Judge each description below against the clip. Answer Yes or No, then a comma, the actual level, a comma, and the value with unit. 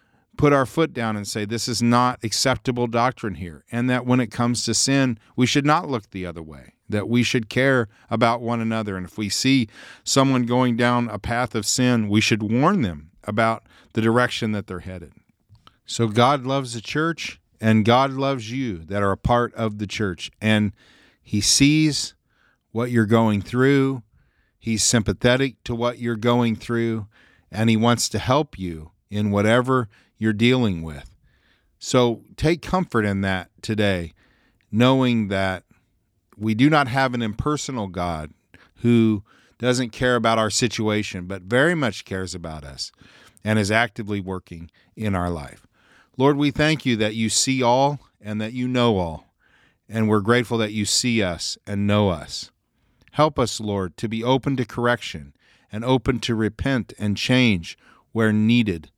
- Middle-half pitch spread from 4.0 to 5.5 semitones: No, average, 3.4 semitones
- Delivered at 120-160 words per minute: No, average, 170 wpm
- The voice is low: Yes, low, 115 Hz